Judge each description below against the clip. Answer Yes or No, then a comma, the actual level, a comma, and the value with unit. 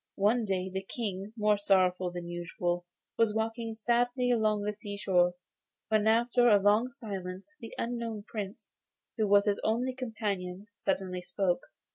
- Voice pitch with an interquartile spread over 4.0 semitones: No, average, 3.2 semitones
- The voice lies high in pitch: Yes, high, 205 Hz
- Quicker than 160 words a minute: No, average, 150 wpm